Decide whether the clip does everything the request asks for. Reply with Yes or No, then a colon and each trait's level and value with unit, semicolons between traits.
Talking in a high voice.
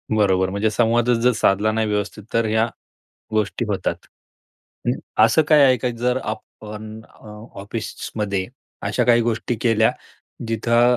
No: low, 110 Hz